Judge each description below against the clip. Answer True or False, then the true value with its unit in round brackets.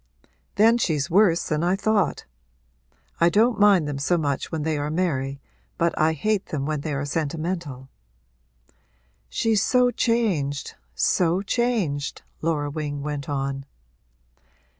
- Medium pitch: True (160 Hz)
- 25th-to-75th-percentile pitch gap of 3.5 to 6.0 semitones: True (5.6 semitones)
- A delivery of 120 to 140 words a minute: True (135 wpm)